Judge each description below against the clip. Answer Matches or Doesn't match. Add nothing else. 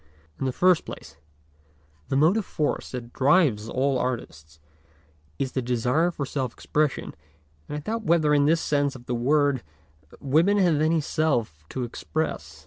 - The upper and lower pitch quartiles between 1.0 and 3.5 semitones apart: Doesn't match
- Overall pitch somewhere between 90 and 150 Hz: Matches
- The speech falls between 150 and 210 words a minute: Matches